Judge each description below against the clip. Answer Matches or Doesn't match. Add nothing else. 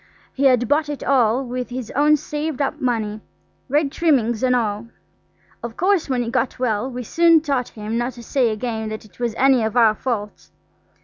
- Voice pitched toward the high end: Matches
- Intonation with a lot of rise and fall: Doesn't match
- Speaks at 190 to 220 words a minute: Matches